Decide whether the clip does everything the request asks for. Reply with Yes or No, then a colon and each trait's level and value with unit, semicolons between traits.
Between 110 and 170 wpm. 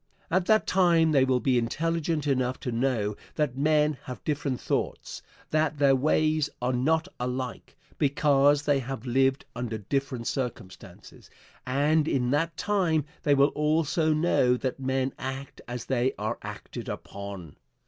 Yes: average, 150 wpm